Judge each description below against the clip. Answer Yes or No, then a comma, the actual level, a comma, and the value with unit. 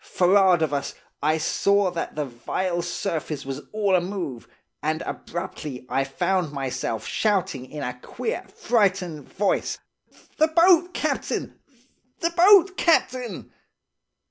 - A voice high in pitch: No, medium, 175 Hz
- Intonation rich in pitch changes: Yes, wide, 6.1 semitones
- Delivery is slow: Yes, slow, 120 wpm